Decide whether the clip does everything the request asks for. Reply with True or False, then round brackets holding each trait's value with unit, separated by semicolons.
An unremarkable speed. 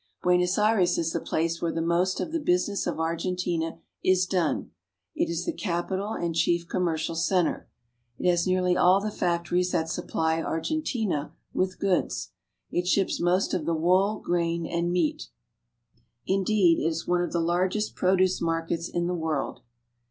True (175 wpm)